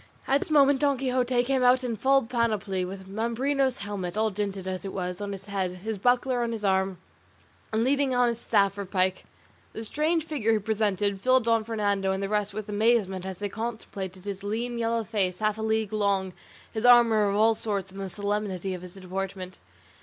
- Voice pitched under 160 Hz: No, high, 210 Hz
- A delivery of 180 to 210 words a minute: Yes, fast, 205 wpm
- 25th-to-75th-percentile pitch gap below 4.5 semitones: Yes, average, 3.4 semitones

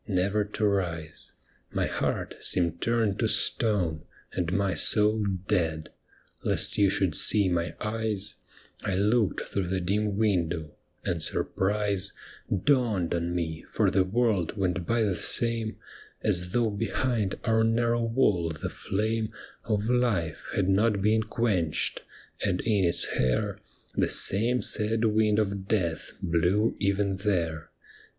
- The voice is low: Yes, low, 100 Hz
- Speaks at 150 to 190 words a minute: No, slow, 135 wpm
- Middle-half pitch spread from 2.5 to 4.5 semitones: Yes, average, 3.7 semitones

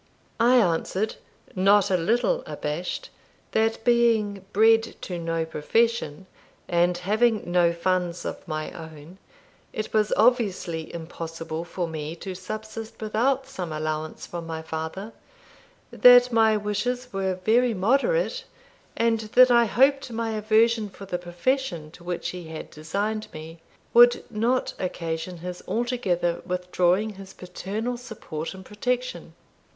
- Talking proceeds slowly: Yes, slow, 130 wpm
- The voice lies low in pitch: No, high, 195 Hz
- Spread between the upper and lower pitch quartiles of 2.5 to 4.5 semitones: No, average, 5.0 semitones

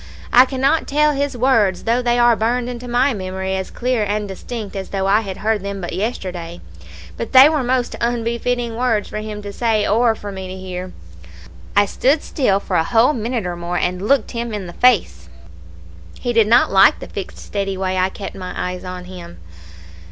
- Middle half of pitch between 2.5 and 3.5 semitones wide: No, average, 4.3 semitones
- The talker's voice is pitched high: Yes, high, 215 Hz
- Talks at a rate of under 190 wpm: No, fast, 205 wpm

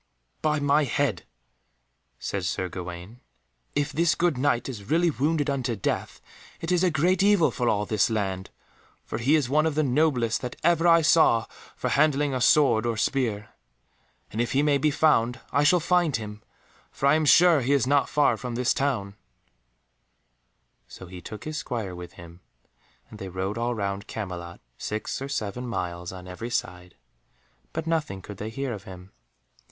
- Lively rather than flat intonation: Yes, wide, 6.8 semitones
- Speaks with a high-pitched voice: No, low, 125 Hz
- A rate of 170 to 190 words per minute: Yes, average, 180 wpm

